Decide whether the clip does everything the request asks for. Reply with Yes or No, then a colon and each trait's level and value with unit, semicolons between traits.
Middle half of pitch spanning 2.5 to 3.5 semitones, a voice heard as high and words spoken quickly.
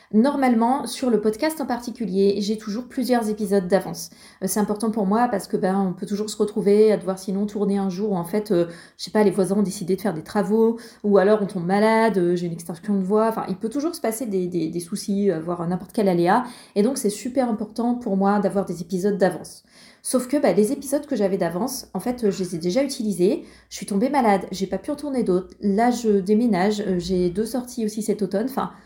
Yes: average, 3.1 semitones; high, 205 Hz; fast, 235 wpm